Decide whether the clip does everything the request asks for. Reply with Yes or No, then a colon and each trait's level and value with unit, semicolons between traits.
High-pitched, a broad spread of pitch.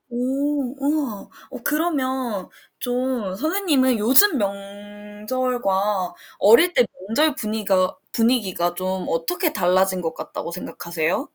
Yes: high, 225 Hz; wide, 5.7 semitones